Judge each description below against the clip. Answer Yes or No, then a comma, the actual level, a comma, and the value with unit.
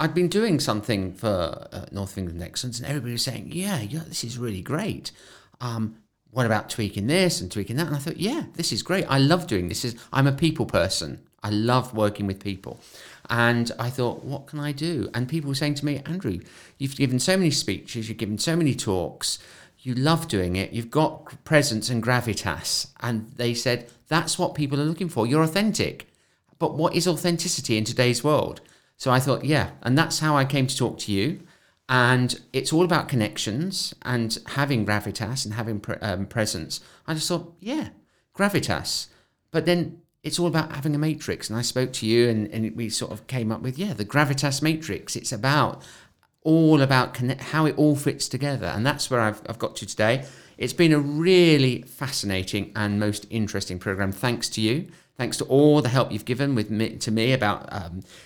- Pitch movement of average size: No, wide, 5.7 semitones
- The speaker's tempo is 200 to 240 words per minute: Yes, fast, 205 wpm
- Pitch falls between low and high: No, low, 125 Hz